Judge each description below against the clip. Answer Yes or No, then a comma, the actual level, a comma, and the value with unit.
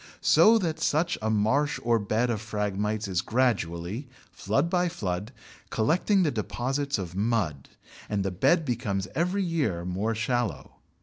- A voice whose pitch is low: Yes, low, 115 Hz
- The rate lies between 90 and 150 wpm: Yes, average, 145 wpm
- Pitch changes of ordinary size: No, wide, 6.6 semitones